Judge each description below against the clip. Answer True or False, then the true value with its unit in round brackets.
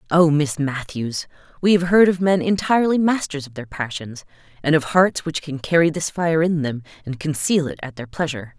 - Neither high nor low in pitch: True (155 Hz)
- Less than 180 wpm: False (205 wpm)